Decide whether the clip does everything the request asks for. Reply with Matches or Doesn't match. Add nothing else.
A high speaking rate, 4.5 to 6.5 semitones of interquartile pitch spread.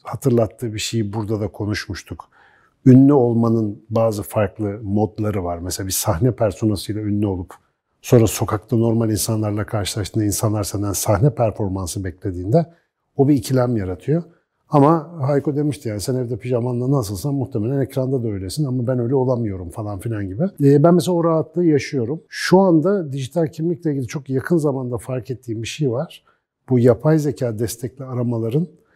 Matches